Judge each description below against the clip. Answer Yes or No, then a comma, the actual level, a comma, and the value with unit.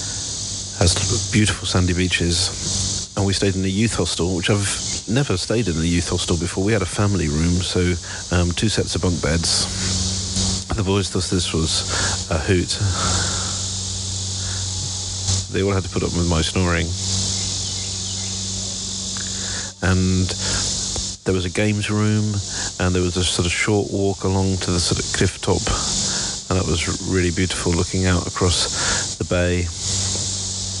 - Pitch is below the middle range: Yes, very low, 95 Hz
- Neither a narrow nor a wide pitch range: No, narrow, 1.1 semitones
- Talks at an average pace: Yes, average, 155 wpm